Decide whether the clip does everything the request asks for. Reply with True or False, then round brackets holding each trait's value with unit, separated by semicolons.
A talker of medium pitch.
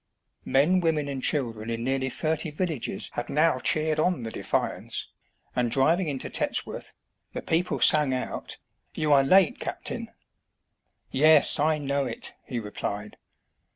True (145 Hz)